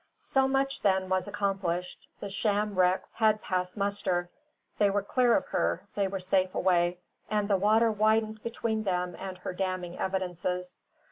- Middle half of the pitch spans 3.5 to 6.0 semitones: No, average, 2.7 semitones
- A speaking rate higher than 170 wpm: No, average, 160 wpm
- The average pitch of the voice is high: Yes, high, 195 Hz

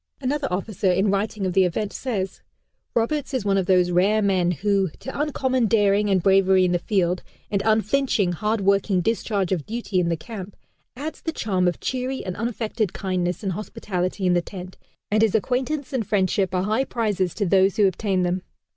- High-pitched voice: Yes, high, 200 Hz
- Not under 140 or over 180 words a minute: No, average, 190 wpm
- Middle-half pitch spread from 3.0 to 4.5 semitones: Yes, average, 3.3 semitones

